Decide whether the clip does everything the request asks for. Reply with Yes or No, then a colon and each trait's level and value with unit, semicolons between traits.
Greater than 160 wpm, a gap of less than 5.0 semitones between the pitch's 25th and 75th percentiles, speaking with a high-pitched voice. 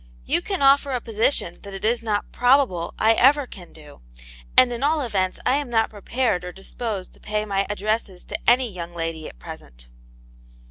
No: average, 190 wpm; wide, 5.4 semitones; high, 215 Hz